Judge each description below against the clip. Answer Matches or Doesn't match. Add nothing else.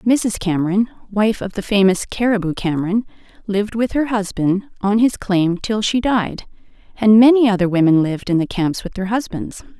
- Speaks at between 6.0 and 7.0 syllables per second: Doesn't match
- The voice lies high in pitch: Matches